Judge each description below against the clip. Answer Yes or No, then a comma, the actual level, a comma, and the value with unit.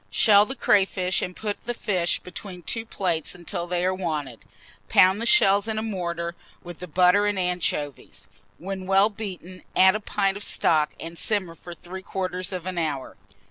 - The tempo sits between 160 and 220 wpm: Yes, average, 180 wpm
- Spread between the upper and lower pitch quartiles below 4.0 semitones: Yes, average, 2.7 semitones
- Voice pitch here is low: No, medium, 185 Hz